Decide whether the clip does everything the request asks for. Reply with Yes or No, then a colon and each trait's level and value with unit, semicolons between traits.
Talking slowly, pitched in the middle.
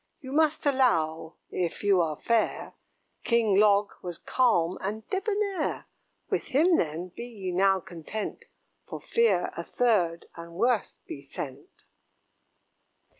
No: slow, 125 wpm; high, 205 Hz